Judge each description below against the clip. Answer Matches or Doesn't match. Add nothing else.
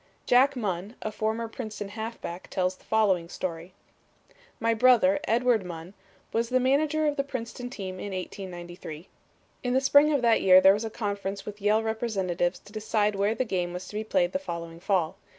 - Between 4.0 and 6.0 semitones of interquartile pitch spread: Matches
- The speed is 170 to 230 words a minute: Matches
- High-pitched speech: Matches